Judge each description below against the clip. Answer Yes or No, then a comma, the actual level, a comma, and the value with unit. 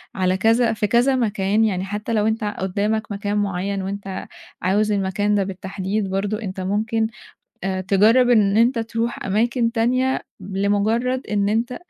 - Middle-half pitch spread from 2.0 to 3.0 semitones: Yes, narrow, 2.6 semitones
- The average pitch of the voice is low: No, high, 210 Hz